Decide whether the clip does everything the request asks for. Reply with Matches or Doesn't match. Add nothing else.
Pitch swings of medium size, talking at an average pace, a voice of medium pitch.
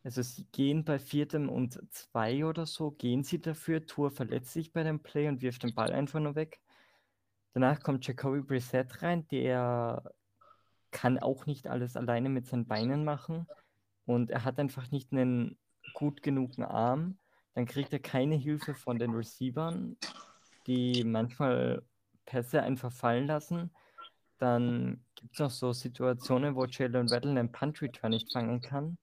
Doesn't match